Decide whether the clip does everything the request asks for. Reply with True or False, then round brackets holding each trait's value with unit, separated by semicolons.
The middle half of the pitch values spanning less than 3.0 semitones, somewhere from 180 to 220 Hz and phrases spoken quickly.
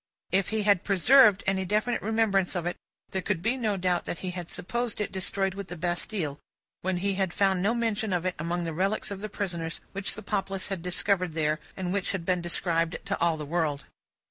True (2.5 semitones; 190 Hz; 215 wpm)